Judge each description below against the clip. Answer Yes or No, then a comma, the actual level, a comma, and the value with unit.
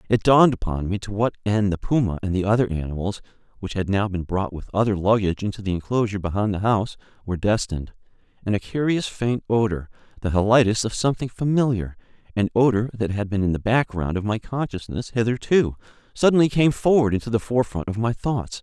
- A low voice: Yes, low, 105 Hz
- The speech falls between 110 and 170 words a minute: No, average, 185 wpm